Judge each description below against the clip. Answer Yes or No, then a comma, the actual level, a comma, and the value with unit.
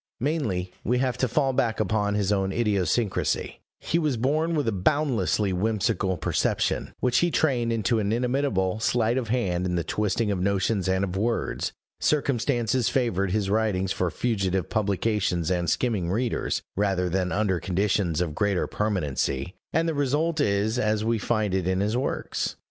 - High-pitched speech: No, low, 105 Hz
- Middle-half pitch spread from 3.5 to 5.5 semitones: Yes, average, 4.5 semitones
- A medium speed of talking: Yes, average, 165 wpm